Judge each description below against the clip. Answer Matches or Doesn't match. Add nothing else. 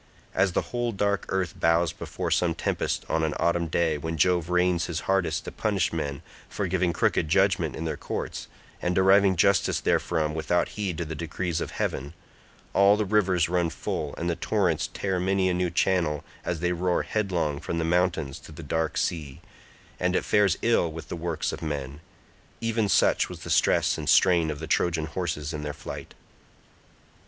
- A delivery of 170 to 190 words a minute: Matches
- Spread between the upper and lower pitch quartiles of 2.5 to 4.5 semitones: Matches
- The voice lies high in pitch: Doesn't match